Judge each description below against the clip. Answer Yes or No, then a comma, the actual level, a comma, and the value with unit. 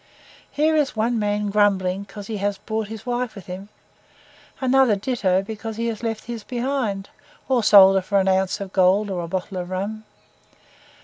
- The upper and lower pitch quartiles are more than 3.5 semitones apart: No, average, 3.0 semitones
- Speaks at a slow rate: No, average, 185 wpm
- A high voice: Yes, high, 205 Hz